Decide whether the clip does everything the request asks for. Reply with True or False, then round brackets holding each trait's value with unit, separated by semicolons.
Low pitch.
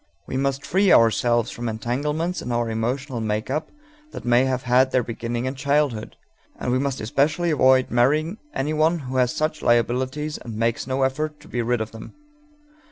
True (130 Hz)